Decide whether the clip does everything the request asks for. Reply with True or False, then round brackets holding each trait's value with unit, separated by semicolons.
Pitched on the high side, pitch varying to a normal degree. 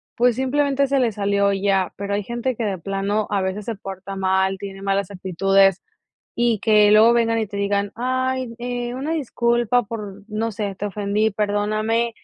True (210 Hz; 3.2 semitones)